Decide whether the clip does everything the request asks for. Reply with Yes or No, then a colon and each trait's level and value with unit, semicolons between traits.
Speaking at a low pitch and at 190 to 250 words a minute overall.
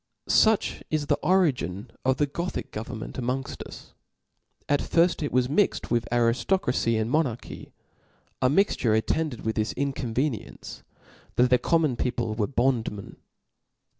No: low, 125 Hz; average, 140 wpm